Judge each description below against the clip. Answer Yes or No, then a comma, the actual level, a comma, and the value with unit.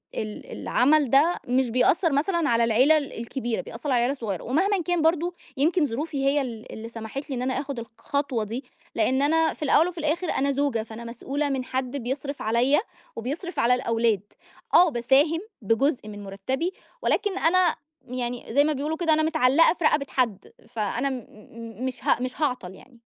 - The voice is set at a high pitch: Yes, very high, 270 Hz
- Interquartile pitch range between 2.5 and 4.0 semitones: No, average, 4.7 semitones